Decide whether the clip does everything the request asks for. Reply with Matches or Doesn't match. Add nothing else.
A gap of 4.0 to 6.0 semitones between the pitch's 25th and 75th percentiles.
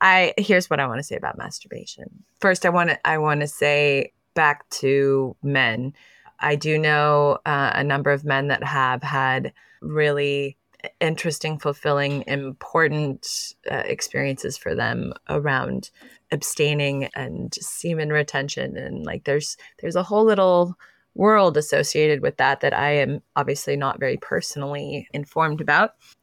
Doesn't match